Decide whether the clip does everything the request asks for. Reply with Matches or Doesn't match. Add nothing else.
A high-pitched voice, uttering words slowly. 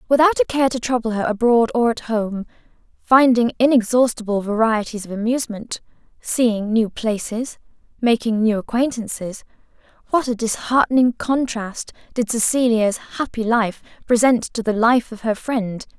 Matches